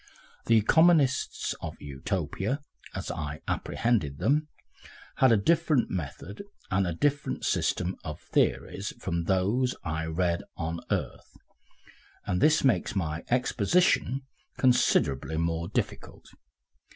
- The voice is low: Yes, very low, 95 Hz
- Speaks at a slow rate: Yes, slow, 120 wpm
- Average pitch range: No, wide, 7.9 semitones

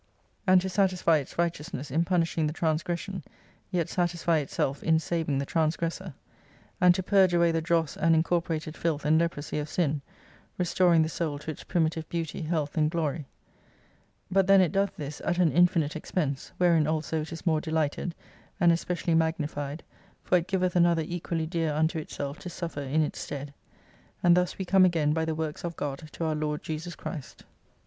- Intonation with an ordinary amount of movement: No, narrow, 2.2 semitones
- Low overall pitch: No, medium, 165 Hz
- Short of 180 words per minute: No, average, 185 wpm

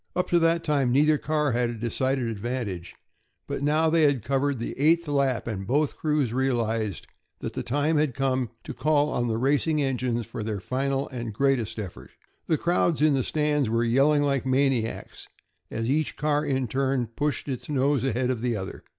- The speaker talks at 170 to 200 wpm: Yes, average, 190 wpm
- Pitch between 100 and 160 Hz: Yes, low, 135 Hz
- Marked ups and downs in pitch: No, average, 3.8 semitones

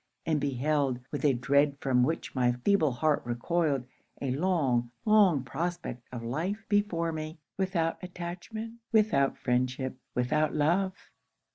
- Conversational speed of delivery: No, slow, 130 wpm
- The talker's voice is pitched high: No, medium, 155 Hz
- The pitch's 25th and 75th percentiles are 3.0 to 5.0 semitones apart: No, wide, 5.4 semitones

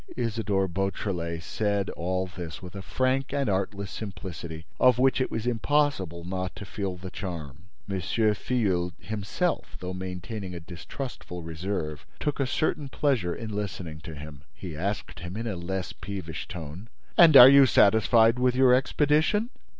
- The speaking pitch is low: Yes, low, 100 Hz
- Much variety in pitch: Yes, wide, 5.8 semitones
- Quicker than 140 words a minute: Yes, average, 160 wpm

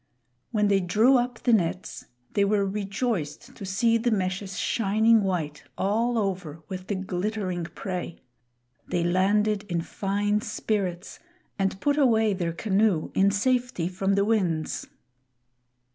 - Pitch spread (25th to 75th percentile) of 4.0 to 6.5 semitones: No, average, 3.1 semitones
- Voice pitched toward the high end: Yes, high, 200 Hz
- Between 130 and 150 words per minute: Yes, slow, 135 wpm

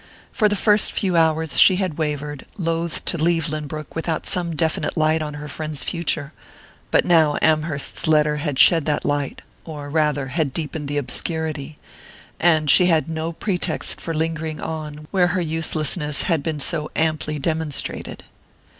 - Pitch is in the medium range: Yes, medium, 155 Hz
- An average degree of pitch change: No, narrow, 1.8 semitones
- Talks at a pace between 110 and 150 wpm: No, average, 160 wpm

